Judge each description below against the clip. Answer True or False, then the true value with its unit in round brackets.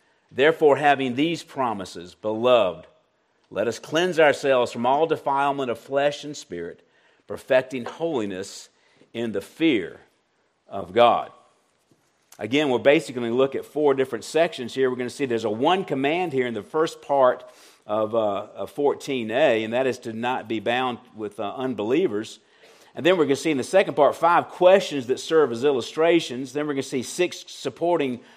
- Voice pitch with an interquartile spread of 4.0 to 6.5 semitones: True (4.6 semitones)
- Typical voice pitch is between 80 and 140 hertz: True (135 Hz)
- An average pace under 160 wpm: False (180 wpm)